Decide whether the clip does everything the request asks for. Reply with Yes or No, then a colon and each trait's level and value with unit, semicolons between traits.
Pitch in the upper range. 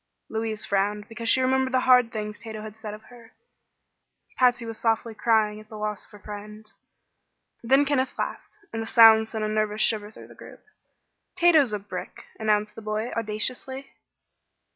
Yes: high, 220 Hz